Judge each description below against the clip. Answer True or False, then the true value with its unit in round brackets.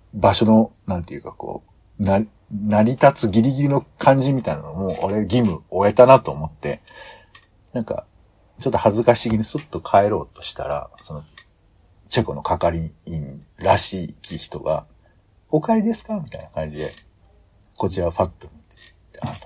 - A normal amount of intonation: True (4.7 semitones)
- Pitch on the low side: True (105 Hz)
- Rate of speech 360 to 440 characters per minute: False (300 characters per minute)